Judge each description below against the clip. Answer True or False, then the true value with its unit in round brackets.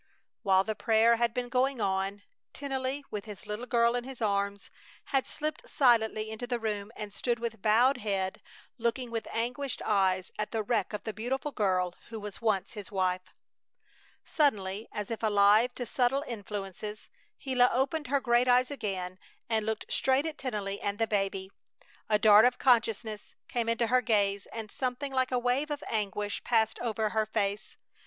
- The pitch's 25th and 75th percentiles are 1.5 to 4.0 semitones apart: True (3.4 semitones)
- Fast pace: False (175 wpm)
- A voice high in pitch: True (225 Hz)